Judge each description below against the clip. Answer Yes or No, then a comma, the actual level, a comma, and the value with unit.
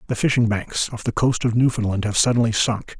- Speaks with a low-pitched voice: Yes, low, 115 Hz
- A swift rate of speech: Yes, fast, 220 wpm